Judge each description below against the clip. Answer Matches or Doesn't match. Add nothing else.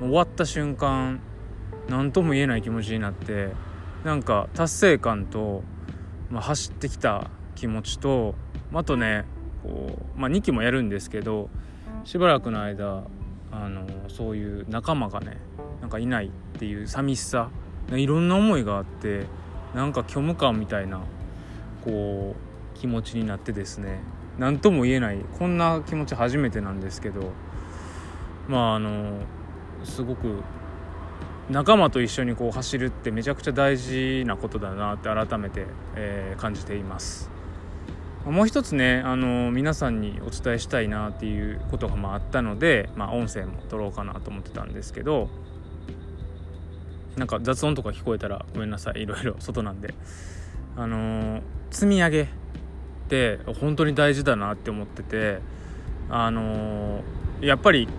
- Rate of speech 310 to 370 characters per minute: Doesn't match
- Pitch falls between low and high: Doesn't match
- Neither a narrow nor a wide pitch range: Matches